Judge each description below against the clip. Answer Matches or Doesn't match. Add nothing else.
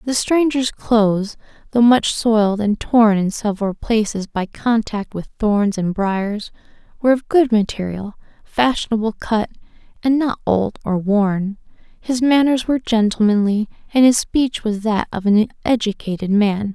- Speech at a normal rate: Matches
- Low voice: Doesn't match